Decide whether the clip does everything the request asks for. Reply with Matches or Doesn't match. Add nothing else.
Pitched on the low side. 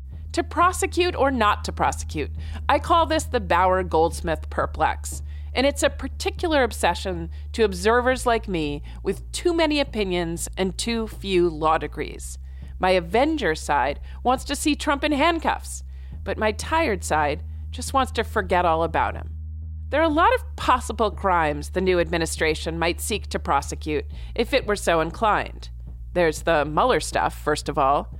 Doesn't match